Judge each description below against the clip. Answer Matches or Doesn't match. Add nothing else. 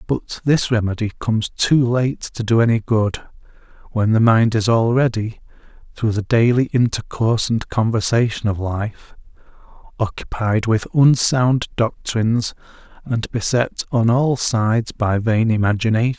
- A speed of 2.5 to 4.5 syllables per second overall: Matches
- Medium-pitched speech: Doesn't match